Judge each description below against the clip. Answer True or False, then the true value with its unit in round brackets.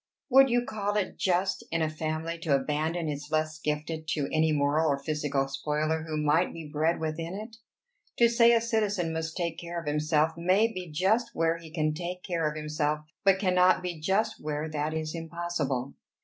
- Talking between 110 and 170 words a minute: False (190 wpm)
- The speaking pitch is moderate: True (160 Hz)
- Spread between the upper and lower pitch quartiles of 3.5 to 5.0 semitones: False (3.0 semitones)